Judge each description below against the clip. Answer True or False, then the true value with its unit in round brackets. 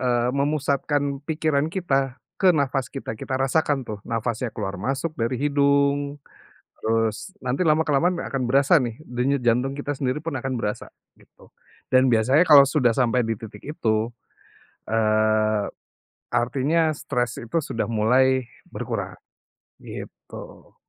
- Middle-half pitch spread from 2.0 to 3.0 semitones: False (3.5 semitones)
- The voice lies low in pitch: True (130 Hz)